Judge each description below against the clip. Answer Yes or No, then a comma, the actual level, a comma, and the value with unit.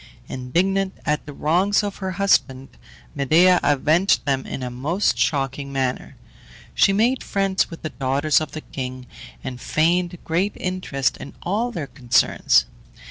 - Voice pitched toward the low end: No, medium, 155 Hz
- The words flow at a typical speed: Yes, average, 145 wpm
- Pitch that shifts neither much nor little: No, wide, 5.7 semitones